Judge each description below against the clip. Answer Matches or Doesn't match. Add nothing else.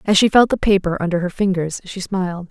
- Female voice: Matches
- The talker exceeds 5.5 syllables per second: Matches